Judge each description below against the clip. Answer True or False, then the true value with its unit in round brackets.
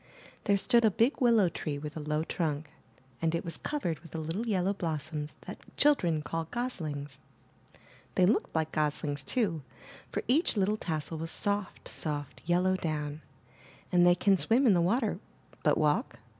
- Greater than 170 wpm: True (180 wpm)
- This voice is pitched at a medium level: True (170 Hz)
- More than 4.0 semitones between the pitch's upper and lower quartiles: True (5.0 semitones)